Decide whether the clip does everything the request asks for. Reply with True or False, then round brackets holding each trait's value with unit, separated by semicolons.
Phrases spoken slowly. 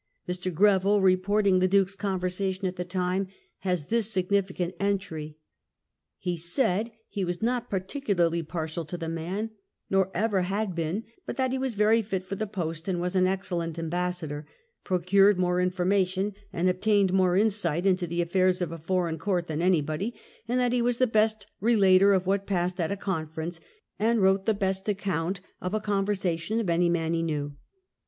False (175 wpm)